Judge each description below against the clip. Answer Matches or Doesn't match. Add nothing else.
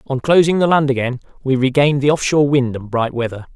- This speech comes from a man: Matches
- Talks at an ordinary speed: Doesn't match